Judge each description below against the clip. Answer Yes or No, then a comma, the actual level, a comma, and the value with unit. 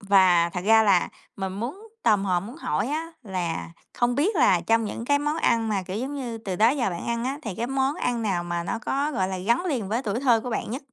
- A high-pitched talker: Yes, high, 225 Hz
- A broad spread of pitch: Yes, wide, 5.7 semitones